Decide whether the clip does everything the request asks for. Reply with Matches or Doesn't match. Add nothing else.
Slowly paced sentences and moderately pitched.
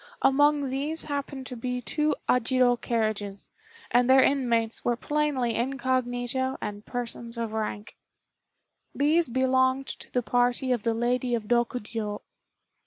Doesn't match